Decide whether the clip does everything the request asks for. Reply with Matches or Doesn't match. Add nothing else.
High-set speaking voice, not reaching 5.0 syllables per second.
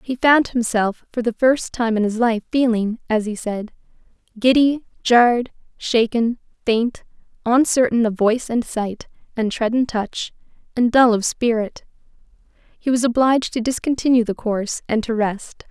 Matches